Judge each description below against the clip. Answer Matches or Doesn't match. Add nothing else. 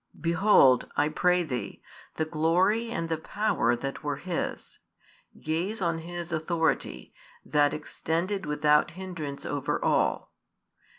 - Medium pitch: Matches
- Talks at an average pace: Doesn't match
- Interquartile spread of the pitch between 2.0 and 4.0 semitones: Matches